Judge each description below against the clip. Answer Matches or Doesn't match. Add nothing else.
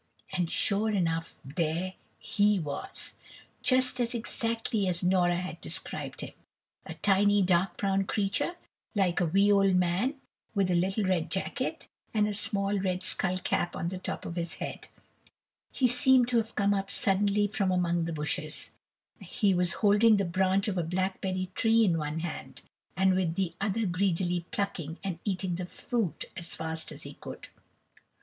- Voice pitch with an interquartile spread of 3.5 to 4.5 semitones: Doesn't match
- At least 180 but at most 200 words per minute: Doesn't match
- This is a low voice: Doesn't match